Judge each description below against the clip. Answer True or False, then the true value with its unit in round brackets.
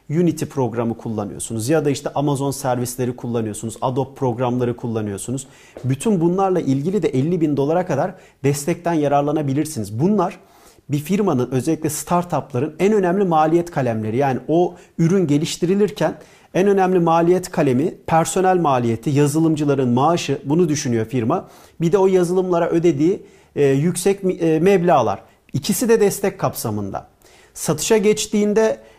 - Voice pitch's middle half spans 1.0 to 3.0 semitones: False (5.6 semitones)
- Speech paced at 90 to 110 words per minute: False (120 wpm)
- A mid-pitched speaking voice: True (155 Hz)